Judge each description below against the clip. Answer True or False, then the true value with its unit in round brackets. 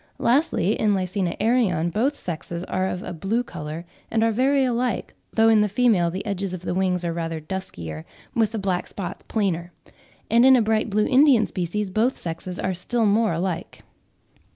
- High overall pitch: True (200 Hz)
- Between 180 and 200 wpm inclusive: True (185 wpm)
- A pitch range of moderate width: True (4.4 semitones)